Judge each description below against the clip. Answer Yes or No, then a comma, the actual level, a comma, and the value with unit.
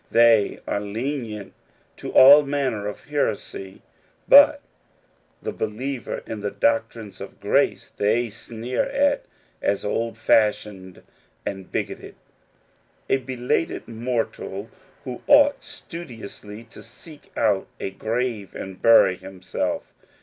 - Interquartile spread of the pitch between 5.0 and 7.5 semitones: No, average, 4.2 semitones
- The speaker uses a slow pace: Yes, slow, 120 wpm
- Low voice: Yes, low, 115 Hz